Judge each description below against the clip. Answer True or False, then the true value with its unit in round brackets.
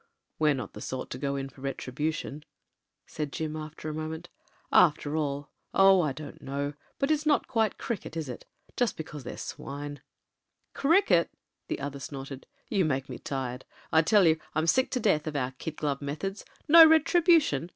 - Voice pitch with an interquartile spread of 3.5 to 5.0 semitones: False (5.6 semitones)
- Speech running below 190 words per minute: False (195 wpm)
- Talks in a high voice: False (155 Hz)